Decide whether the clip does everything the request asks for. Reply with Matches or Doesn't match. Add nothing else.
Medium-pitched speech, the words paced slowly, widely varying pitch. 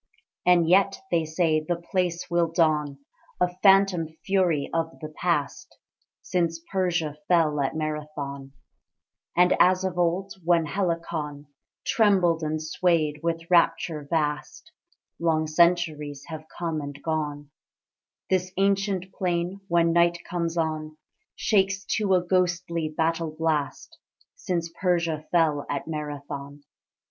Doesn't match